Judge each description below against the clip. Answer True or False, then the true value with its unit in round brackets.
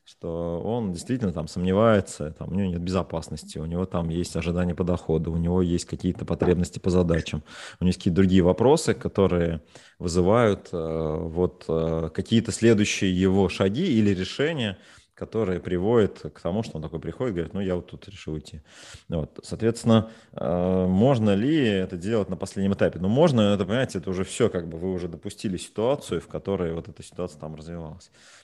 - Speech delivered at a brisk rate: True (175 wpm)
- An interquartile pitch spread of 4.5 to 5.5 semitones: False (2.7 semitones)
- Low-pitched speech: True (90 Hz)